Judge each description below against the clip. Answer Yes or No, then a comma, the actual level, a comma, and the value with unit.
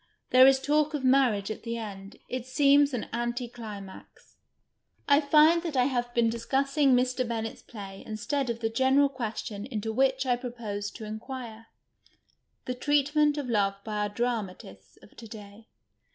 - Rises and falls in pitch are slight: No, average, 3.8 semitones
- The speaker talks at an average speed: Yes, average, 165 wpm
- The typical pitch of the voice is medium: No, high, 240 Hz